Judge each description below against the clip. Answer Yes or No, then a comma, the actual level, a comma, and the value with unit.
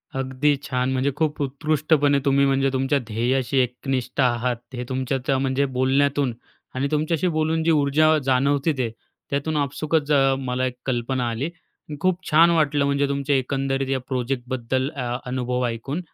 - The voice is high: No, low, 135 Hz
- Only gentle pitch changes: Yes, narrow, 2.1 semitones